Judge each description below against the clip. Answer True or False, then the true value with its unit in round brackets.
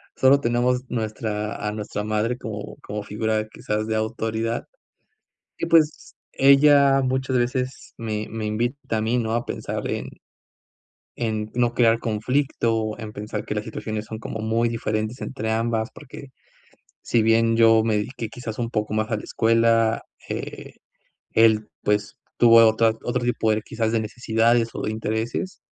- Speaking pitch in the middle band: False (115 Hz)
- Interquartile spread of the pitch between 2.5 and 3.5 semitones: False (1.9 semitones)